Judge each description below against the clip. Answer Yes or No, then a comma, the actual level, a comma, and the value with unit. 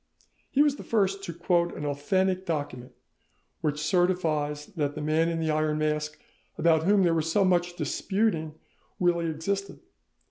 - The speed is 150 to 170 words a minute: Yes, average, 155 wpm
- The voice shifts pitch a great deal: No, average, 3.6 semitones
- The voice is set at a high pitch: No, medium, 165 Hz